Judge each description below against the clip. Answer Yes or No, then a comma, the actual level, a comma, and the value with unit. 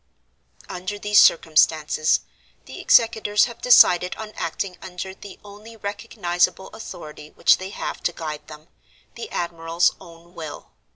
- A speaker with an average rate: No, slow, 125 wpm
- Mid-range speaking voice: Yes, medium, 180 Hz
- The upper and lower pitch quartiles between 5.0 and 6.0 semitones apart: No, average, 3.9 semitones